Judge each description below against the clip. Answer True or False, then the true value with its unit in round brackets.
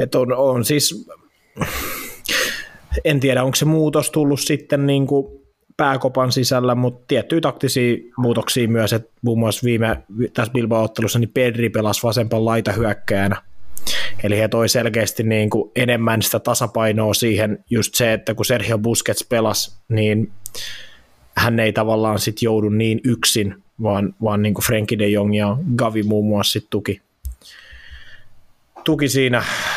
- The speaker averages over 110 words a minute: True (135 wpm)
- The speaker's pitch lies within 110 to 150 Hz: True (115 Hz)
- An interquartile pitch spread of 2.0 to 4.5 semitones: True (2.9 semitones)